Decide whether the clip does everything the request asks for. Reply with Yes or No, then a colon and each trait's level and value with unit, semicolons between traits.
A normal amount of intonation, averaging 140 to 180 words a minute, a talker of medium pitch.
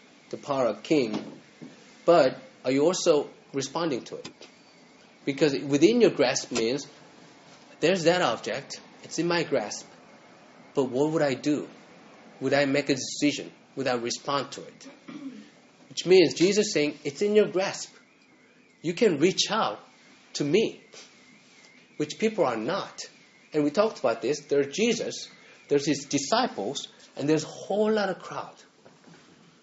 No: wide, 6.7 semitones; average, 150 wpm; medium, 155 Hz